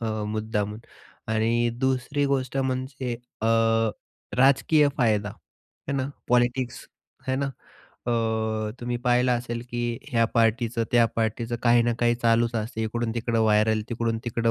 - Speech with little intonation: Yes, narrow, 1.8 semitones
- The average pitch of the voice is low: Yes, low, 120 Hz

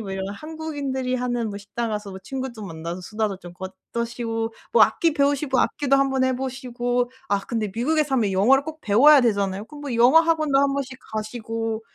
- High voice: Yes, high, 245 Hz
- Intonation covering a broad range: No, average, 4.3 semitones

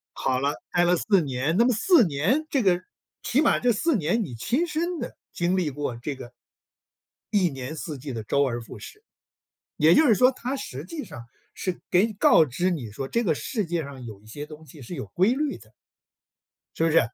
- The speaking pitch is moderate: Yes, medium, 170 Hz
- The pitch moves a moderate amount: No, wide, 8.9 semitones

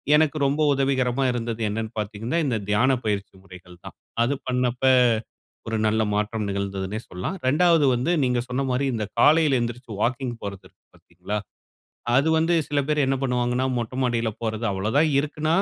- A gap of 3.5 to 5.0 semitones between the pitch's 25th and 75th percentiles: Yes, average, 4.2 semitones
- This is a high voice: No, low, 120 Hz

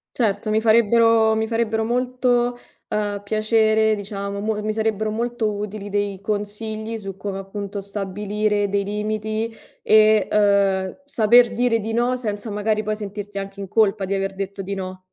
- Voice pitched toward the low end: No, high, 215 Hz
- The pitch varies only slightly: Yes, narrow, 1.7 semitones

